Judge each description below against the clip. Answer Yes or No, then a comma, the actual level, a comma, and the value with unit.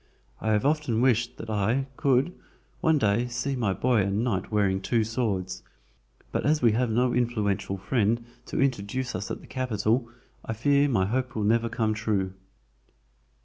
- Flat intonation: No, average, 3.6 semitones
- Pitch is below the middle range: Yes, low, 115 Hz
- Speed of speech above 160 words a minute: Yes, average, 170 wpm